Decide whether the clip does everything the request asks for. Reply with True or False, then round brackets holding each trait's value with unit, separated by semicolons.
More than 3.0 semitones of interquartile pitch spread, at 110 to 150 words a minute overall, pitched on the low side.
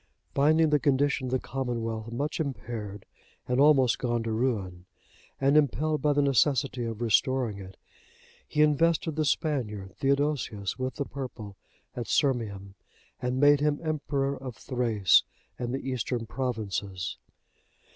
True (4.1 semitones; 135 wpm; 130 Hz)